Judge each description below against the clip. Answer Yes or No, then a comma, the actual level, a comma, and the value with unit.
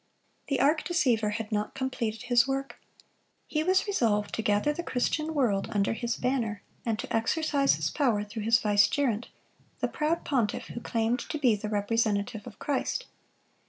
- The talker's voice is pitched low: No, high, 235 Hz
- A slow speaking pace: No, average, 165 wpm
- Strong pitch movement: No, average, 4.7 semitones